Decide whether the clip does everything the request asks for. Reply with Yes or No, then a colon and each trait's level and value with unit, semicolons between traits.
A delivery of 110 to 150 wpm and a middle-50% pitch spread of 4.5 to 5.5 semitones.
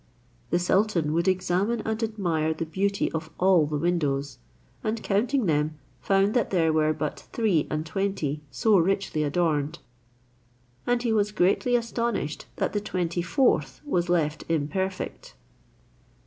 Yes: average, 140 wpm; average, 4.9 semitones